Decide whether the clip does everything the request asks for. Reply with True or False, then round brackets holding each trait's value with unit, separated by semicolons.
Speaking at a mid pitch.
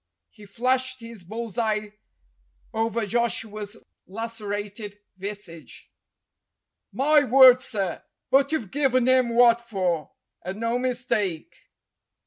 False (230 Hz)